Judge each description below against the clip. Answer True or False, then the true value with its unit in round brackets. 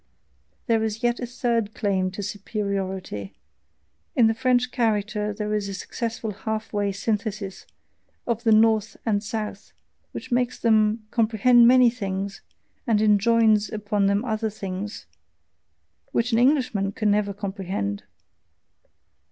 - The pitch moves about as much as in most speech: False (2.3 semitones)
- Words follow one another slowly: True (130 wpm)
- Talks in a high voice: True (215 Hz)